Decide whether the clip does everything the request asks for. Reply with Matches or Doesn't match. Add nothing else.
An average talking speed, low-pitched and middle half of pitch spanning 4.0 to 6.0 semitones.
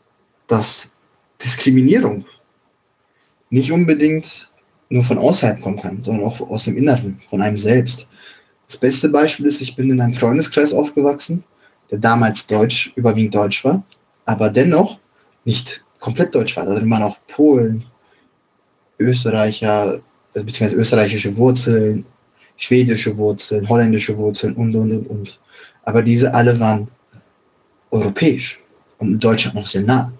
Doesn't match